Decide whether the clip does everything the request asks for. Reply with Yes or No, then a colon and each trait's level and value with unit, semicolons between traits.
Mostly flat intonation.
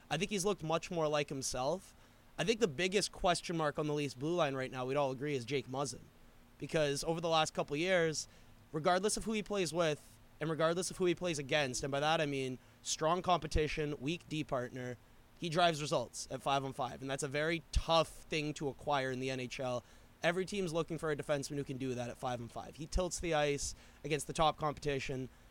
No: average, 3.8 semitones